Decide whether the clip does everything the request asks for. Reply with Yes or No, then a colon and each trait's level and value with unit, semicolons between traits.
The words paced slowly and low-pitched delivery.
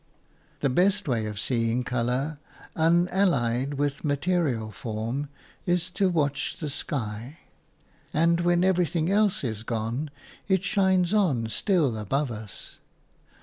No: slow, 120 wpm; medium, 145 Hz